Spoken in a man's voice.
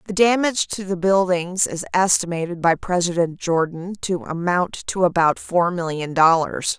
No: female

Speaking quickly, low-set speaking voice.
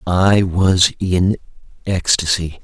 No: slow, 90 wpm; very low, 90 Hz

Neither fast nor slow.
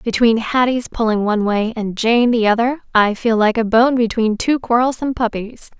Yes: average, 185 wpm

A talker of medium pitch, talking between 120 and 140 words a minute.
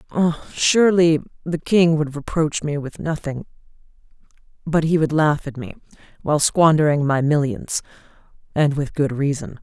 Yes: medium, 150 Hz; slow, 135 wpm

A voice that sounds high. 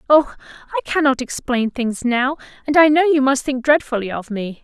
Yes: very high, 260 Hz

